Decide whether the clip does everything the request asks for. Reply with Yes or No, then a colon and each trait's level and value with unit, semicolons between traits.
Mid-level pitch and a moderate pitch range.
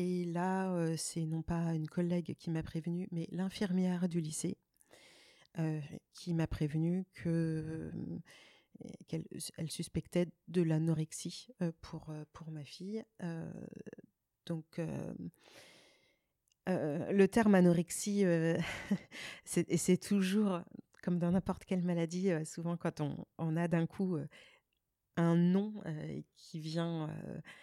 No: medium, 170 Hz; narrow, 2.3 semitones